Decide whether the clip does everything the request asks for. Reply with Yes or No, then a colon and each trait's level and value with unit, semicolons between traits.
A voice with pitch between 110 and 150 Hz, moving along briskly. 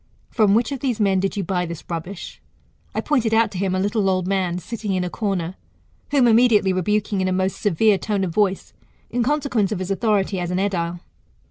No: high, 195 Hz; fast, 215 wpm